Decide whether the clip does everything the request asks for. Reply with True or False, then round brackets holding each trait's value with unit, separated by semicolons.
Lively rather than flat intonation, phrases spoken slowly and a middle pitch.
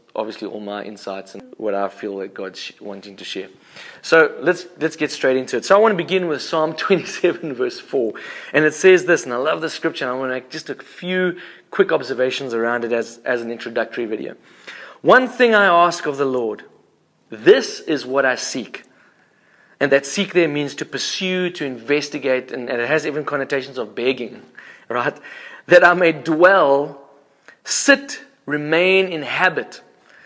False (5.7 semitones; 185 wpm; 150 Hz)